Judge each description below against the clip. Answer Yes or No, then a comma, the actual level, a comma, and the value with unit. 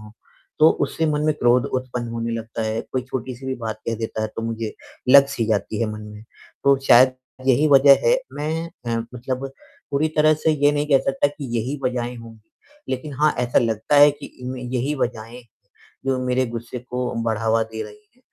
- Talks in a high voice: No, low, 125 Hz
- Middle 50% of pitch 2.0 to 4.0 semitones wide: Yes, average, 3.5 semitones